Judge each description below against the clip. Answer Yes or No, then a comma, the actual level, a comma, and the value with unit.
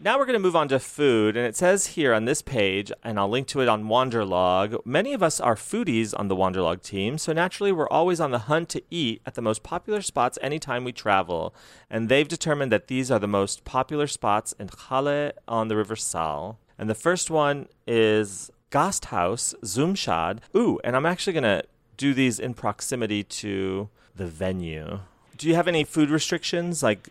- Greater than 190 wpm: Yes, average, 200 wpm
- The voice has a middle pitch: No, low, 125 Hz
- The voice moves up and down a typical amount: No, wide, 6.7 semitones